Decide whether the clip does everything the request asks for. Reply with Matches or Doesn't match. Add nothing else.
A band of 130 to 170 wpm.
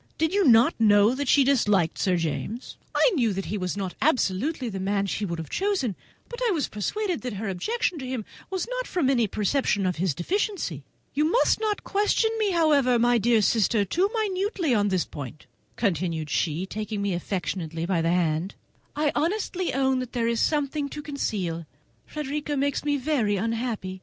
Doesn't match